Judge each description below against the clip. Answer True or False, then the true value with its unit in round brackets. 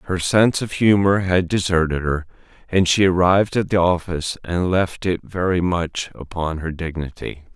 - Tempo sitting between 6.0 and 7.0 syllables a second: False (4.8 syllables/s)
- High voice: False (90 Hz)